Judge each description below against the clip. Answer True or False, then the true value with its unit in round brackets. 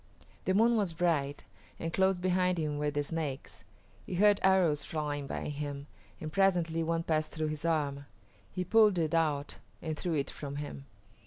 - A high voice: False (160 Hz)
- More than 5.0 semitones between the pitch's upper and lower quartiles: False (3.6 semitones)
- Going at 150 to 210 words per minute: True (175 wpm)